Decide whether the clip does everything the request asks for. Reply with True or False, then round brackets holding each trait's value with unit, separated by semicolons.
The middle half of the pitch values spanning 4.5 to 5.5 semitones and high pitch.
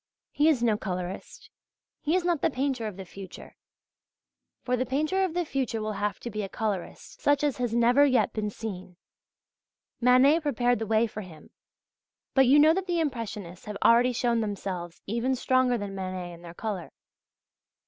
True (5.2 semitones; 235 Hz)